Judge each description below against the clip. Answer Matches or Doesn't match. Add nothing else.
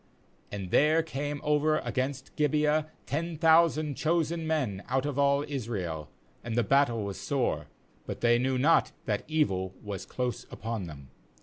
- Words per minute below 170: Matches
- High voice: Doesn't match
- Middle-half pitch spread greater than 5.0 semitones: Matches